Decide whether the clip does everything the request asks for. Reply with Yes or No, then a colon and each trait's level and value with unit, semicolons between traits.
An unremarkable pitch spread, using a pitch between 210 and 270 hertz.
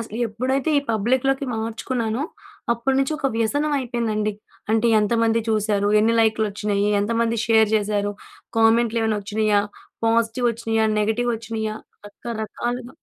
No: narrow, 1.8 semitones; high, 225 Hz